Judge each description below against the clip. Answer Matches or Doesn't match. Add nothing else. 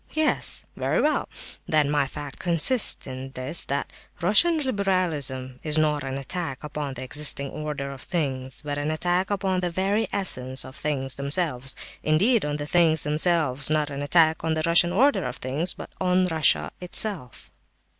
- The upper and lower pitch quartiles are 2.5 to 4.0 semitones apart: Doesn't match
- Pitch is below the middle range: Doesn't match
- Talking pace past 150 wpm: Matches